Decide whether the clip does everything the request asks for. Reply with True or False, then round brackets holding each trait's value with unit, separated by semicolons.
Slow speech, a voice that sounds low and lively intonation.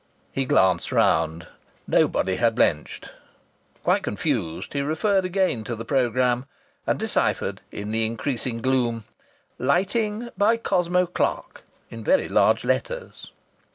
True (120 wpm; 130 Hz; 8.4 semitones)